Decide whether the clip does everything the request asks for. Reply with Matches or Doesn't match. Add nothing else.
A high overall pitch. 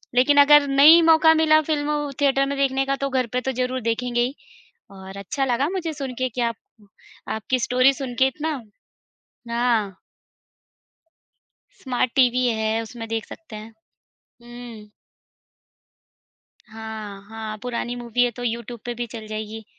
Matches